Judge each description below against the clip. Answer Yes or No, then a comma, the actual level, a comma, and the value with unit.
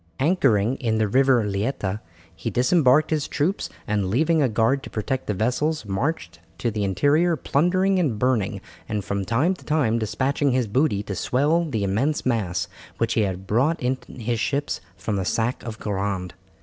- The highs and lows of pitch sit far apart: Yes, wide, 5.7 semitones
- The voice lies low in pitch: Yes, low, 120 Hz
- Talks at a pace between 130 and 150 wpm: No, average, 175 wpm